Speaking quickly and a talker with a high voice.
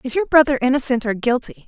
Yes: fast, 215 wpm; very high, 260 Hz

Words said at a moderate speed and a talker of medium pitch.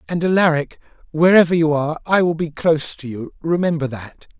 Yes: average, 180 wpm; medium, 155 Hz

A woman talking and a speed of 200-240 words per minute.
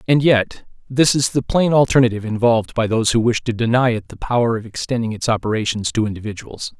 No: male; fast, 205 wpm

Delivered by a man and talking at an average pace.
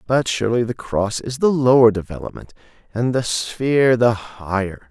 Yes: male; average, 160 wpm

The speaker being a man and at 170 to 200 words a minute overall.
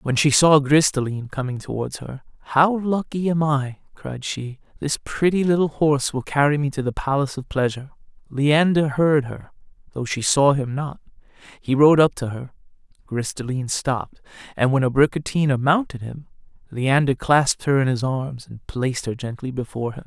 Yes: male; average, 180 wpm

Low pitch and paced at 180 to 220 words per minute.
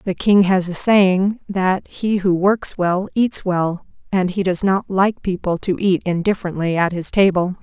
No: medium, 185 Hz; average, 190 wpm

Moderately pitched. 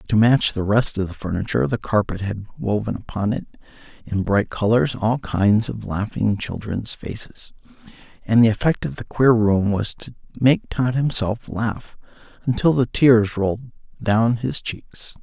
No: low, 110 Hz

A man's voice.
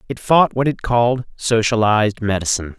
Yes: male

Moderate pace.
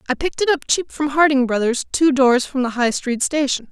No: fast, 240 wpm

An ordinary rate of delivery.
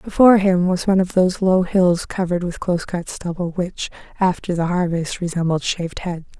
Yes: average, 190 wpm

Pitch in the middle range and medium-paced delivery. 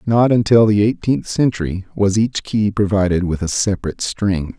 No: low, 105 Hz; average, 170 wpm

